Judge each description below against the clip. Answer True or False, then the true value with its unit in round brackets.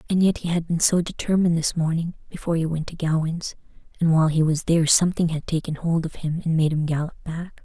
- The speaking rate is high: True (235 wpm)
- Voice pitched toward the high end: False (165 Hz)